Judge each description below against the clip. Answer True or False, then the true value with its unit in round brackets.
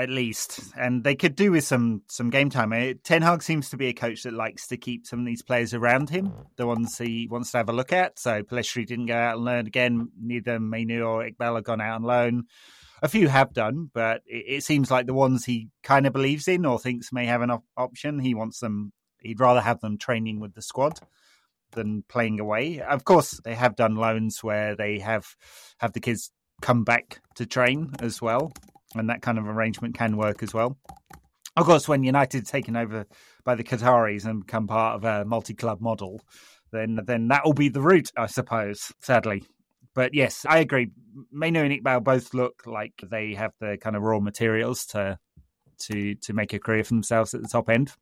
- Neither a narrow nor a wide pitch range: False (2.3 semitones)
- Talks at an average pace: False (220 wpm)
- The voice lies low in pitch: True (120 Hz)